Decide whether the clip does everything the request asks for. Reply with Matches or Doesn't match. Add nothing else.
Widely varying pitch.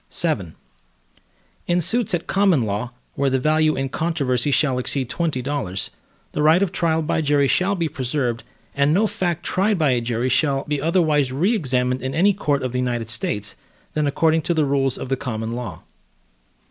Doesn't match